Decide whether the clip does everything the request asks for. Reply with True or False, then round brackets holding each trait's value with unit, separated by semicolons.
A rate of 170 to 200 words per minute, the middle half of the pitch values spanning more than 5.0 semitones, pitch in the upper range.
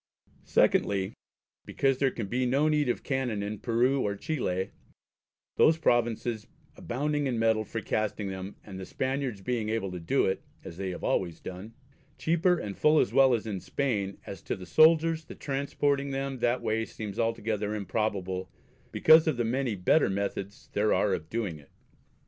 False (180 wpm; 5.4 semitones; 115 Hz)